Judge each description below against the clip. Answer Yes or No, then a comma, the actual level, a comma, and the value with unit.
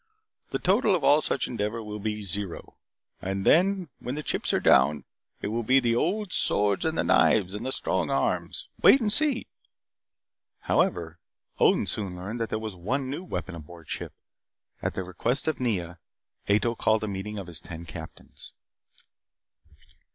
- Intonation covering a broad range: Yes, wide, 6.5 semitones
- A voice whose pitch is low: Yes, low, 105 Hz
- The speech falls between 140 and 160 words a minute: No, average, 175 wpm